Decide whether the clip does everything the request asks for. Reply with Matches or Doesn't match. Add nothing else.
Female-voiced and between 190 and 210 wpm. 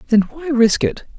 Matches